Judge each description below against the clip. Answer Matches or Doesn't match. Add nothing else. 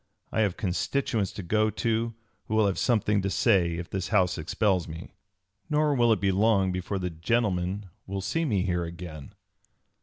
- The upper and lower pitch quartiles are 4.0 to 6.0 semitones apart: Doesn't match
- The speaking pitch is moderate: Doesn't match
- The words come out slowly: Doesn't match